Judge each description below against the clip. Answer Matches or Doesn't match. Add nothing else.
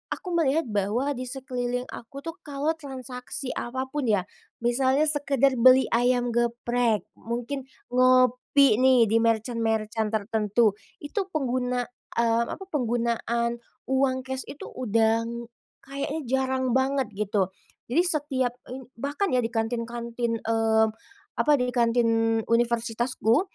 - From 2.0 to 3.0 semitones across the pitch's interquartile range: Matches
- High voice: Matches